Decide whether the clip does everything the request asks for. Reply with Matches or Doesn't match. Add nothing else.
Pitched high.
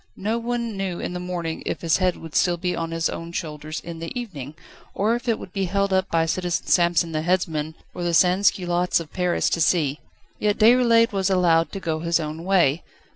Doesn't match